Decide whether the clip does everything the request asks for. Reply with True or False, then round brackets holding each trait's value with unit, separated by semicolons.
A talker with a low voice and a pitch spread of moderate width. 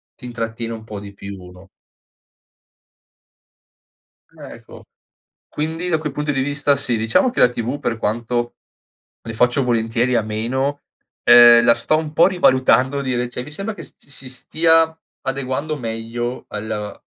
True (125 Hz; 4.0 semitones)